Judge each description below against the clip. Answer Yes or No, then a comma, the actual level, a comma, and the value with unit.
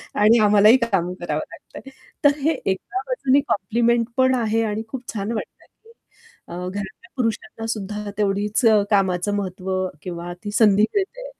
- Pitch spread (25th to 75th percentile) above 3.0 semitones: Yes, average, 3.4 semitones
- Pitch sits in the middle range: No, high, 210 Hz